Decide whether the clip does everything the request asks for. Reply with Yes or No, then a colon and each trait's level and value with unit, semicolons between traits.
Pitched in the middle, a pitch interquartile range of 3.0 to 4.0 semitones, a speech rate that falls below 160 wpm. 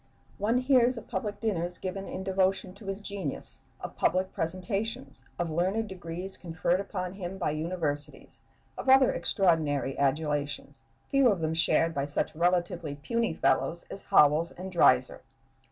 Yes: medium, 180 Hz; average, 3.5 semitones; average, 150 wpm